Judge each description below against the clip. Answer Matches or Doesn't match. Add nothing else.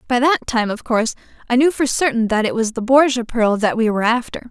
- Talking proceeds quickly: Matches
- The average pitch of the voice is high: Matches